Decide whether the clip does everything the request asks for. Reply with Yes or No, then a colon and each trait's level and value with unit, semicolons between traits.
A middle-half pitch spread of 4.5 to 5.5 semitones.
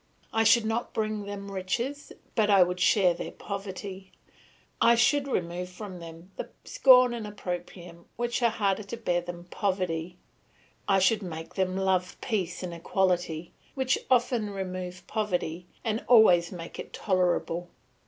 No: average, 3.6 semitones